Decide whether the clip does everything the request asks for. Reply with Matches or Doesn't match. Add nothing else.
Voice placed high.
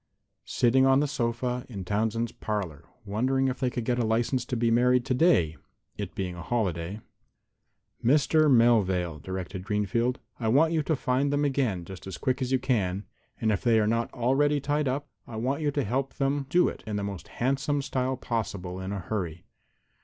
Doesn't match